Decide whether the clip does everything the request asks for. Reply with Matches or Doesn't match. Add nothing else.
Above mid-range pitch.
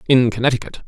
Doesn't match